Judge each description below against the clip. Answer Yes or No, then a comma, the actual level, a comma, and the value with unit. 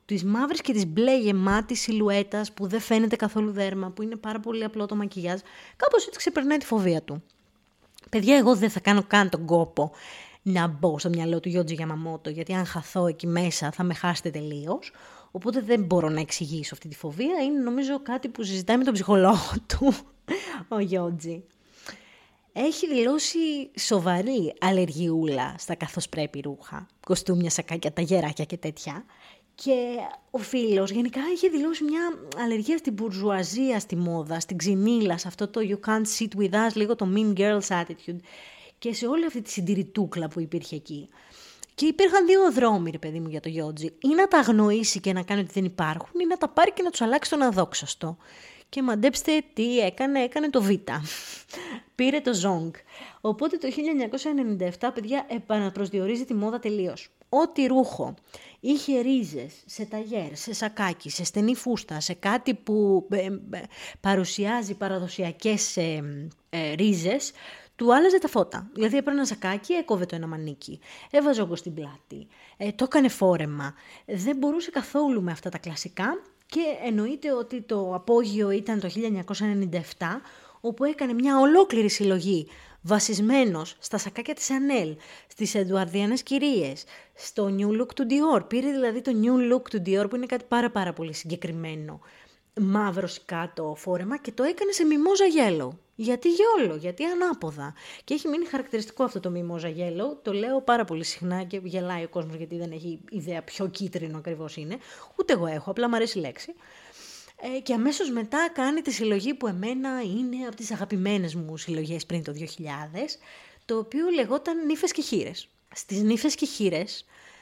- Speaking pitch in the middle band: No, high, 210 Hz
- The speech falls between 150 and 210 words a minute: Yes, average, 165 wpm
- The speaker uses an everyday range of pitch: No, wide, 6.7 semitones